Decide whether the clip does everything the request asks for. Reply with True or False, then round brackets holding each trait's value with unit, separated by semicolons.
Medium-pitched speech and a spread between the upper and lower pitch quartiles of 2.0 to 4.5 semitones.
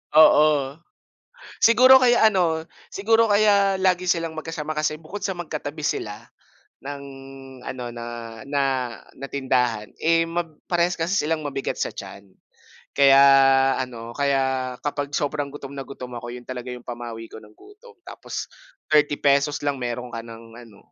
False (145 Hz; 5.0 semitones)